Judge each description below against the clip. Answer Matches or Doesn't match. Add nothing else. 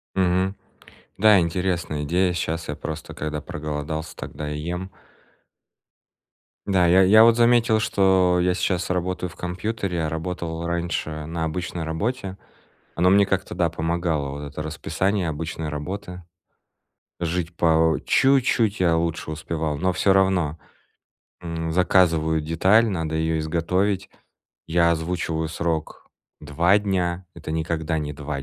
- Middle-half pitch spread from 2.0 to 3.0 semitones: Matches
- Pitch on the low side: Matches